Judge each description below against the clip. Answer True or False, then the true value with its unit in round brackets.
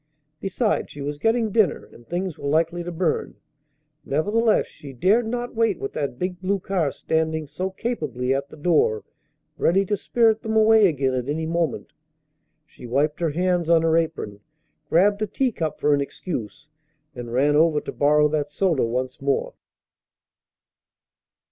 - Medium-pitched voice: True (160 Hz)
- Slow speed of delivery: False (160 wpm)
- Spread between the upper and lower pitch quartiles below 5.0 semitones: False (5.3 semitones)